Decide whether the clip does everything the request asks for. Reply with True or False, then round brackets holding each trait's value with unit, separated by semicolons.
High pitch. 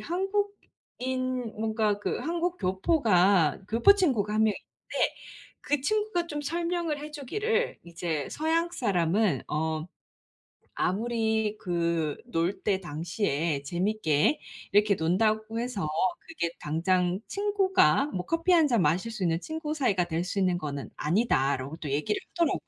True (215 Hz)